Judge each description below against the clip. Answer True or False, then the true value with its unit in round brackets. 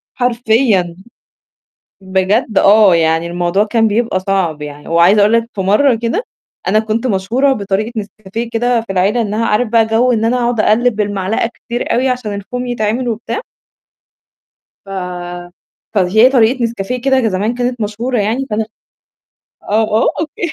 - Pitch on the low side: False (220 Hz)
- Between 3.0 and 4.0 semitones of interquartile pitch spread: True (3.5 semitones)